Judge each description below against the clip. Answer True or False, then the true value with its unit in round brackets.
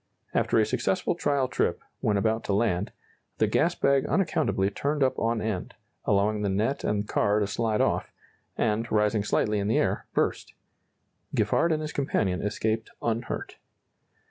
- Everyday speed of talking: True (160 wpm)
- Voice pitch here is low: True (110 Hz)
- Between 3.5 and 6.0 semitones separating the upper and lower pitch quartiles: True (4.0 semitones)